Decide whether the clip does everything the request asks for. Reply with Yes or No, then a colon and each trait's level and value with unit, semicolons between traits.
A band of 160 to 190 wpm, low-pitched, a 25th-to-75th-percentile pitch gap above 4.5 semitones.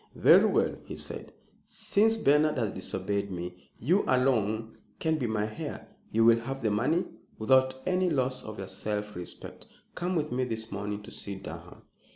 Yes: average, 175 wpm; low, 115 Hz; average, 5.2 semitones